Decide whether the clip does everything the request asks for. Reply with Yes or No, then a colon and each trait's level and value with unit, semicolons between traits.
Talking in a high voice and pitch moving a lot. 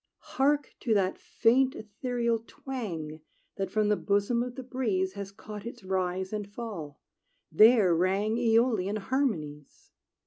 No: high, 210 Hz; average, 4.1 semitones